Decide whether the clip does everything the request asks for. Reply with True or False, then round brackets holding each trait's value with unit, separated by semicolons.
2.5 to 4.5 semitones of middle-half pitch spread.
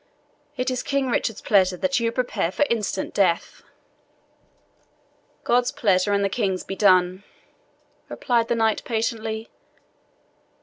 True (3.7 semitones)